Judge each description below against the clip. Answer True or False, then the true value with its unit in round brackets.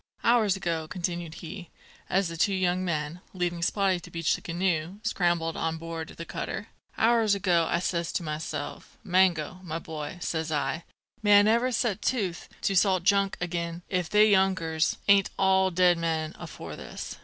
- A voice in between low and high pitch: True (175 Hz)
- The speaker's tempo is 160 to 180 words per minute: True (170 wpm)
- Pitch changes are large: False (2.7 semitones)